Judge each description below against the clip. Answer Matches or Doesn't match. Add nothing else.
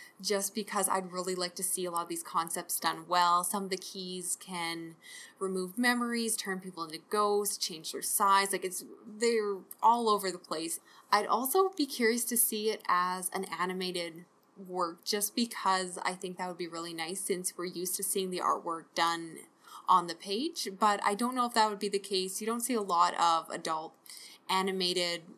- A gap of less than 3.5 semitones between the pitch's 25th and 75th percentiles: Matches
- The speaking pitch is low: Doesn't match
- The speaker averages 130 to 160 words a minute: Doesn't match